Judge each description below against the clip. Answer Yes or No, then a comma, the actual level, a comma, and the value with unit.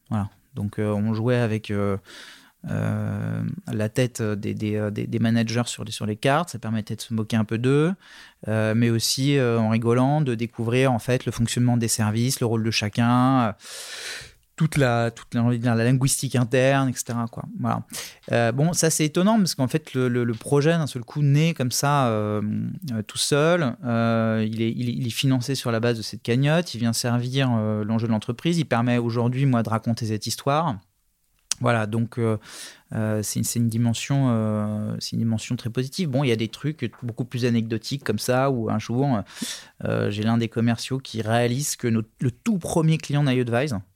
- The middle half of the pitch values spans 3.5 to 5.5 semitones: No, average, 3.0 semitones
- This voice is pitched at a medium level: No, low, 120 Hz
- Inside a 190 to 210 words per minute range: Yes, average, 200 wpm